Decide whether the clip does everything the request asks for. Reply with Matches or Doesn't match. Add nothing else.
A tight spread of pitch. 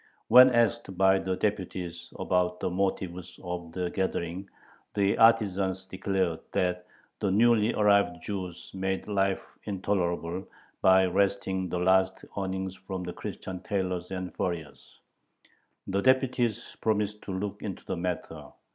Matches